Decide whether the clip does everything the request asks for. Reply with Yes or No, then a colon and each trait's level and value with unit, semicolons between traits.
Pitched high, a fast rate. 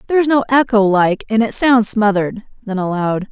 No: high, 220 Hz; average, 180 wpm